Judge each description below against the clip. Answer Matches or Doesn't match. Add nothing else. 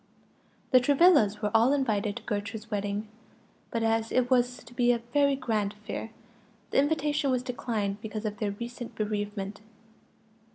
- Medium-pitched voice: Doesn't match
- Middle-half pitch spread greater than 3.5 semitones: Doesn't match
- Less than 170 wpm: Matches